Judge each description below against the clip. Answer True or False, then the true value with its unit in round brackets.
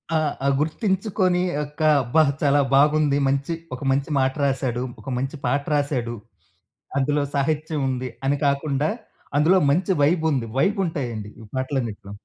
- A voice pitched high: False (140 Hz)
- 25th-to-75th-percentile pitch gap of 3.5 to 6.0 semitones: False (2.9 semitones)